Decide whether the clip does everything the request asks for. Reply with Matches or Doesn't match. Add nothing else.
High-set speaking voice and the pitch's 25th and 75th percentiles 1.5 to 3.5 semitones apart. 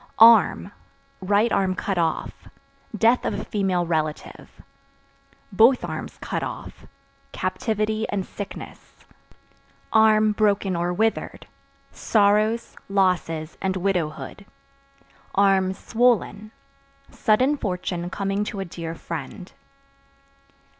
Matches